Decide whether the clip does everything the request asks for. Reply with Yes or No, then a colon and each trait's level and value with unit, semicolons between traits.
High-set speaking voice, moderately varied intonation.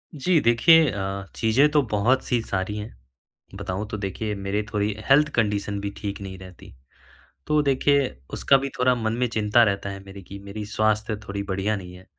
No: low, 105 Hz; average, 3.8 semitones